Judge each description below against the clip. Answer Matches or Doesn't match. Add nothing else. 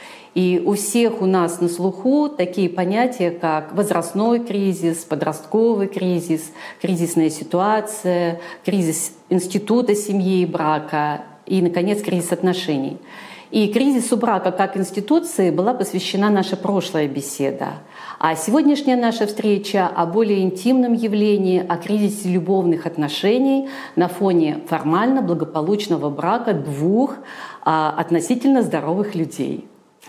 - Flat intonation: Doesn't match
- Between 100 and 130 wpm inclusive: Matches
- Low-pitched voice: Doesn't match